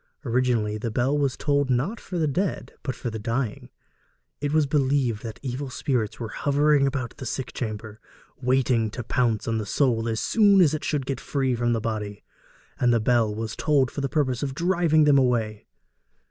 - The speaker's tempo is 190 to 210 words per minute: Yes, average, 195 wpm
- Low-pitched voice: Yes, low, 130 Hz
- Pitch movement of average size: Yes, average, 3.9 semitones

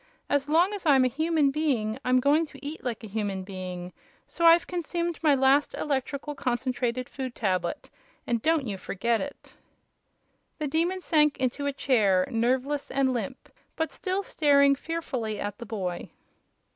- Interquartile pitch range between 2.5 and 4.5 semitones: No, average, 5.0 semitones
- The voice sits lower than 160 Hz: No, very high, 270 Hz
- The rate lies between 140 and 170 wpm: Yes, average, 160 wpm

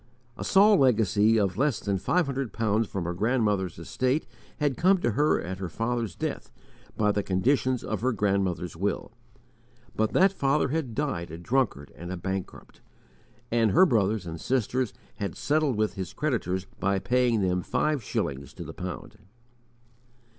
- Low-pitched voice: Yes, low, 110 Hz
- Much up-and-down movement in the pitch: Yes, wide, 5.7 semitones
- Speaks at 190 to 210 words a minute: No, average, 165 wpm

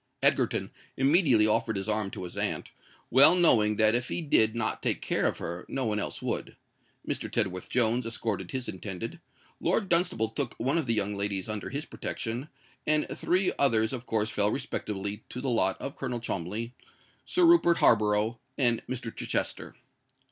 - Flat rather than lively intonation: No, average, 4.2 semitones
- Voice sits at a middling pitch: No, low, 115 Hz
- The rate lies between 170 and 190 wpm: Yes, average, 175 wpm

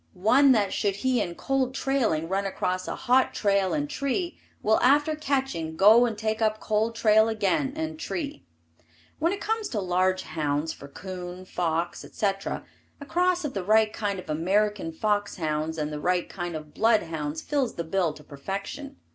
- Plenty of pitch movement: Yes, wide, 6.9 semitones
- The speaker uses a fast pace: No, average, 180 wpm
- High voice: Yes, high, 205 Hz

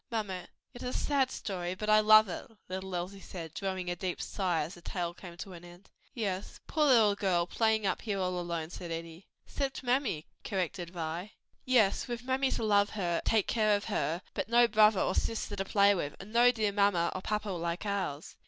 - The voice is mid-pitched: No, high, 195 Hz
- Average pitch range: Yes, average, 3.6 semitones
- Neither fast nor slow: No, fast, 210 wpm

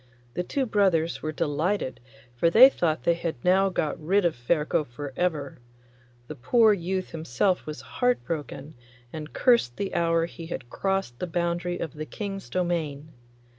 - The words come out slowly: No, average, 165 wpm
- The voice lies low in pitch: No, medium, 170 Hz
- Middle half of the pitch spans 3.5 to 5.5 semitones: Yes, average, 3.9 semitones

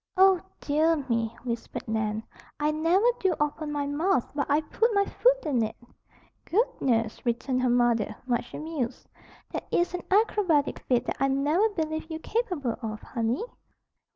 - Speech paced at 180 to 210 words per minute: No, average, 155 wpm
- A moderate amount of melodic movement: No, wide, 6.3 semitones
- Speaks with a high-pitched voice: Yes, very high, 290 Hz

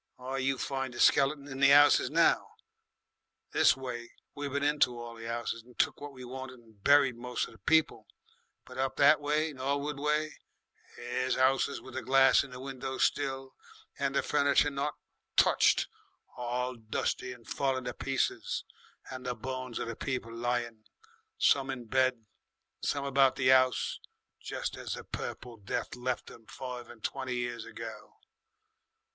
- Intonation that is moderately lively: No, narrow, 2.2 semitones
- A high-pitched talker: No, low, 130 Hz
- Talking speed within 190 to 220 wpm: No, average, 165 wpm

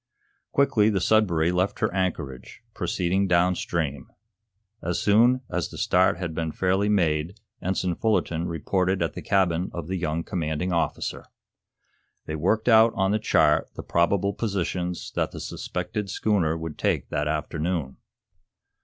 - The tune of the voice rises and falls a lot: No, average, 3.3 semitones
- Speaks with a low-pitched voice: Yes, very low, 90 Hz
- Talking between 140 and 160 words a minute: Yes, average, 145 wpm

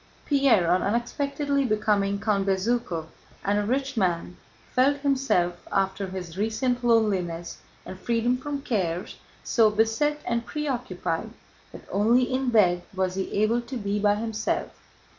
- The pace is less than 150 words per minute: Yes, average, 140 wpm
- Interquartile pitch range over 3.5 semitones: Yes, average, 4.7 semitones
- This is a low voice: No, high, 215 Hz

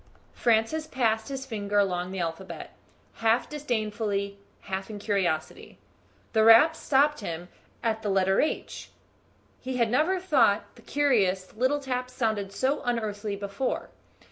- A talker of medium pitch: No, high, 220 Hz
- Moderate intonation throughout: Yes, average, 4.5 semitones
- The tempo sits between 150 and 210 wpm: No, slow, 135 wpm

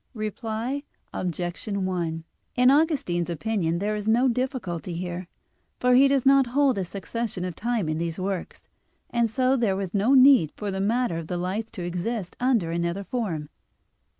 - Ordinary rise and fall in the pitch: No, wide, 5.9 semitones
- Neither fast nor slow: Yes, average, 170 wpm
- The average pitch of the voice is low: No, high, 205 Hz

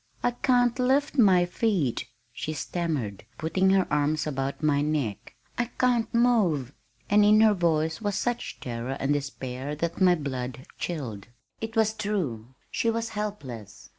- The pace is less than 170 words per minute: Yes, average, 150 wpm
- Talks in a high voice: No, medium, 165 Hz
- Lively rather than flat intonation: Yes, wide, 7.8 semitones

